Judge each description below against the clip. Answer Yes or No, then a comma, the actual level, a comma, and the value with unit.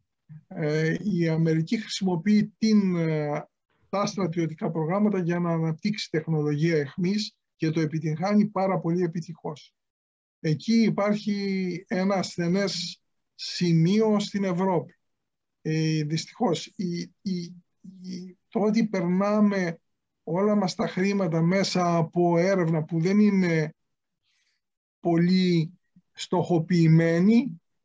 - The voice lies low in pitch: No, medium, 180 Hz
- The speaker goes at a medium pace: No, slow, 95 wpm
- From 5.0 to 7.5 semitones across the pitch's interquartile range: No, average, 3.3 semitones